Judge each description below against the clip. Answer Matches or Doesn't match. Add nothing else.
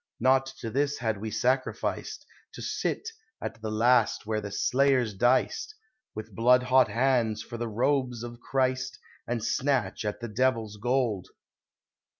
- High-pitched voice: Doesn't match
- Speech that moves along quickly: Doesn't match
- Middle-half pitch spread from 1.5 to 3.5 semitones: Matches